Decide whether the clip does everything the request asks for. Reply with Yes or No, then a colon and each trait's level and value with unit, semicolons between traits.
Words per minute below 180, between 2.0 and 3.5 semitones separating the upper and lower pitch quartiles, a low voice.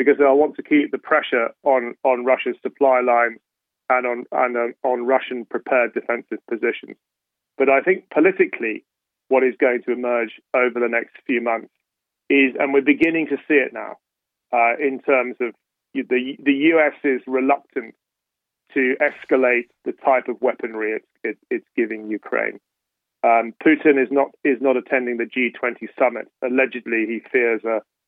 Yes: average, 165 wpm; narrow, 2.6 semitones; low, 130 Hz